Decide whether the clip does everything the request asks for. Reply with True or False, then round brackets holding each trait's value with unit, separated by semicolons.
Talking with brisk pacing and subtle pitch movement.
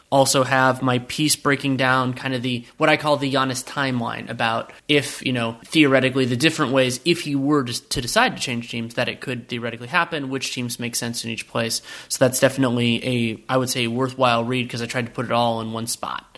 True (230 wpm; 2.2 semitones)